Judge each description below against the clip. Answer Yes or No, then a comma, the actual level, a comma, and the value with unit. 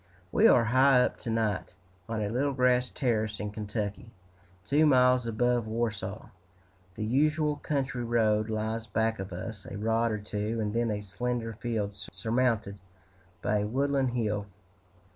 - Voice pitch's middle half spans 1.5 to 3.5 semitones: Yes, average, 2.9 semitones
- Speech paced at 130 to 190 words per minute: Yes, average, 155 wpm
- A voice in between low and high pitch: No, low, 115 Hz